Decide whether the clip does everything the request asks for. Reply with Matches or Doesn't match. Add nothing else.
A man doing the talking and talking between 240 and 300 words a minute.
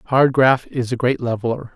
Doesn't match